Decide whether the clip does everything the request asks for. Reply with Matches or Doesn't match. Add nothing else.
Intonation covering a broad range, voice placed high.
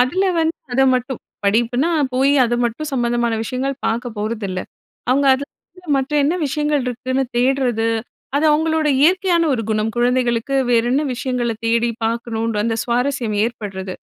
Doesn't match